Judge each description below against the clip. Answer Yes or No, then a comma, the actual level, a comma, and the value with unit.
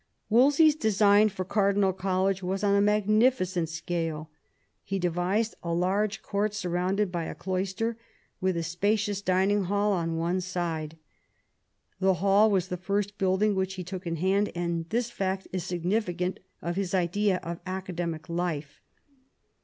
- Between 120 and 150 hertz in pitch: No, high, 190 Hz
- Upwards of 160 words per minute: No, average, 155 wpm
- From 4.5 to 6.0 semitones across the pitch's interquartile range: No, average, 2.7 semitones